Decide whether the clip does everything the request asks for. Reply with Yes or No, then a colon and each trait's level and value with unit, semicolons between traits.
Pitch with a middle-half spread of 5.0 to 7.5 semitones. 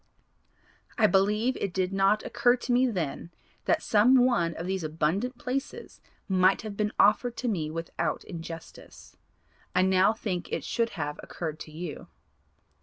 Yes: average, 5.3 semitones